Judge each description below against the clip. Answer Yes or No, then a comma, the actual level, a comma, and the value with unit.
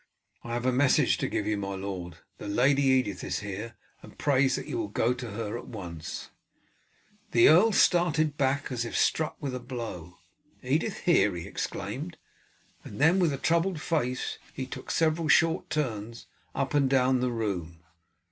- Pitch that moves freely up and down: Yes, wide, 5.7 semitones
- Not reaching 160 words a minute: No, average, 175 wpm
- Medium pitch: No, low, 130 Hz